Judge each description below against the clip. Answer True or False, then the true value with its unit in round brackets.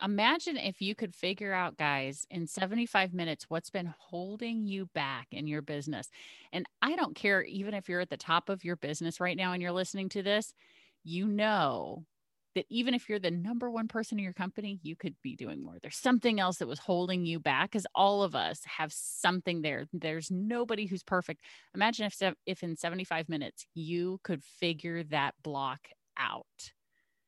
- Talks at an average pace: True (190 wpm)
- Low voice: False (180 Hz)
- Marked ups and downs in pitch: False (3.8 semitones)